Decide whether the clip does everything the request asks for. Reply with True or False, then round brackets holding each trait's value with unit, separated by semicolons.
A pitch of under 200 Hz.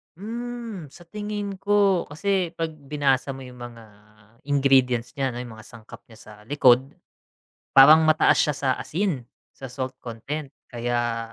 True (140 Hz)